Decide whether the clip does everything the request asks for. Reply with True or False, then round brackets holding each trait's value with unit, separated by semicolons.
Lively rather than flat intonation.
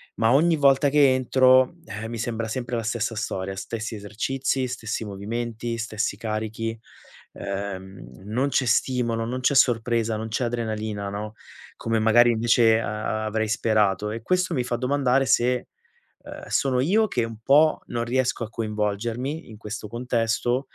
False (2.7 semitones)